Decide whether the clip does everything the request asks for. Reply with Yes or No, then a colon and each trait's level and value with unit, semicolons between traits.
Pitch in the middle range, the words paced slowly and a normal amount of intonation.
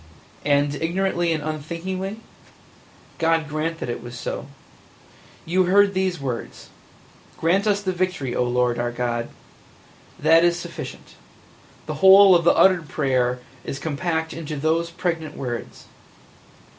Yes: medium, 165 Hz; slow, 130 wpm; average, 4.6 semitones